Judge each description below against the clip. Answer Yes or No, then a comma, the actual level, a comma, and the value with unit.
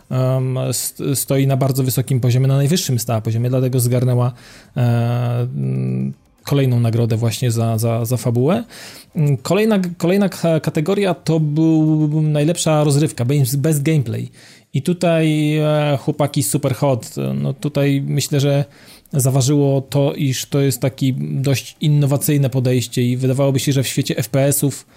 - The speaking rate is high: No, average, 125 wpm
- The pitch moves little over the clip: No, average, 3.2 semitones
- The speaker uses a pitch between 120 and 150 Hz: Yes, low, 135 Hz